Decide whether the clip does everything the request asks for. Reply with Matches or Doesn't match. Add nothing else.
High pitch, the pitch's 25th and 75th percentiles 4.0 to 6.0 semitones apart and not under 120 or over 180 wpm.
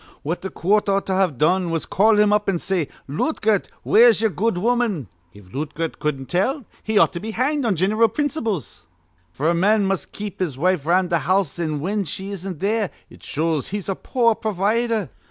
Doesn't match